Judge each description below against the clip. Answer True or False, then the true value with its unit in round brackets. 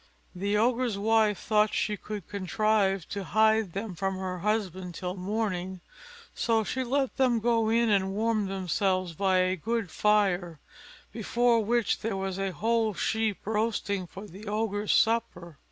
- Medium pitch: False (210 Hz)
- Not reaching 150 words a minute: False (155 wpm)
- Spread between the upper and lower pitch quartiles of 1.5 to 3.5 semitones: True (2.9 semitones)